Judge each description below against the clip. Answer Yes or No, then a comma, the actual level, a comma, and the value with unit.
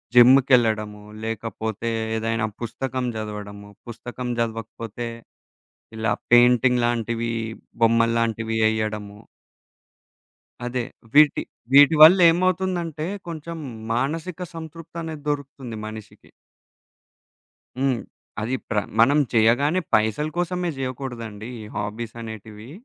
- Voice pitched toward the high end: No, low, 120 Hz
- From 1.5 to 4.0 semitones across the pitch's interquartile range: No, average, 4.5 semitones